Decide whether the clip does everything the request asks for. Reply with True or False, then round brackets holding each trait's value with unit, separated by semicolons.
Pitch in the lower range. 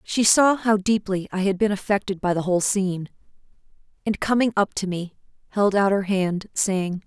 False (195 Hz)